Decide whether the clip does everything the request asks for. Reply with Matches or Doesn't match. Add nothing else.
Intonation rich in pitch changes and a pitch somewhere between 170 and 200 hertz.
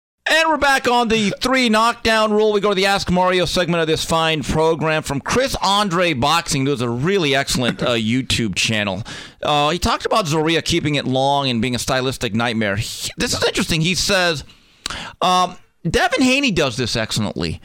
Doesn't match